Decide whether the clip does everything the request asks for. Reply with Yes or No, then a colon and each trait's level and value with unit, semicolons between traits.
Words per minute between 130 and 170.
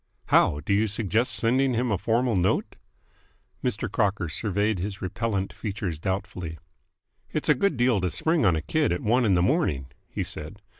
No: average, 180 wpm